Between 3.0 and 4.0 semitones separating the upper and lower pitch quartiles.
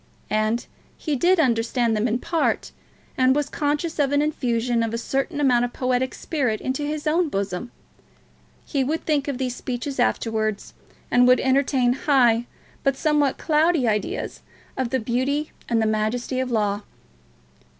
Yes: average, 3.7 semitones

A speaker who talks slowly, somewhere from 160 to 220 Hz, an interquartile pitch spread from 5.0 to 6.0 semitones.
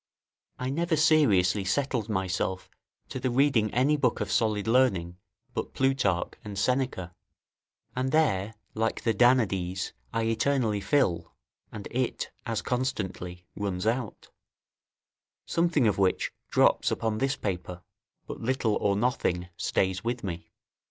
No: slow, 130 wpm; low, 110 Hz; wide, 5.4 semitones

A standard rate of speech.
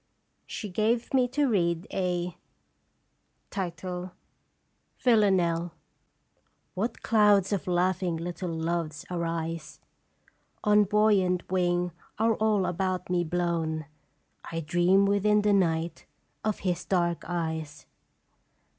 No: slow, 100 wpm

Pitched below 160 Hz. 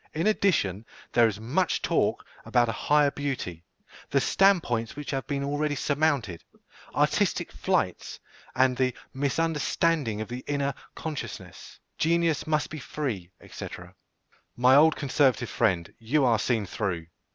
Yes: low, 135 Hz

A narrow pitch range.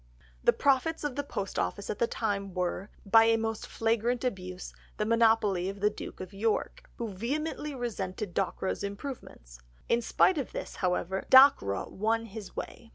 No: average, 3.7 semitones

